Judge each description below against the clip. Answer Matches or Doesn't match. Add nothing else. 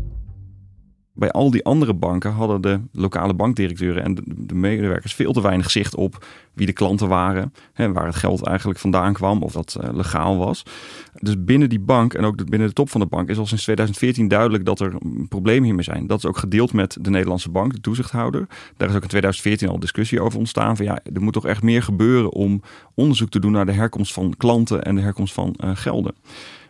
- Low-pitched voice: Matches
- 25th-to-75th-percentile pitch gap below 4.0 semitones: Matches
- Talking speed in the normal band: Doesn't match